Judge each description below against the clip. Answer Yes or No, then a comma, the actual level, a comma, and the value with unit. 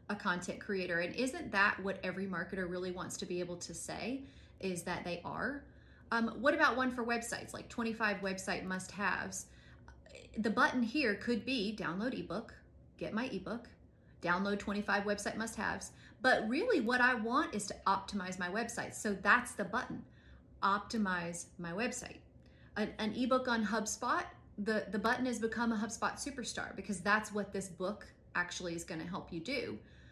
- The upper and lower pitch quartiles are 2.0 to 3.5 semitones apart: No, average, 4.3 semitones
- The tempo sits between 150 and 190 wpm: Yes, average, 170 wpm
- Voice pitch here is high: Yes, high, 205 Hz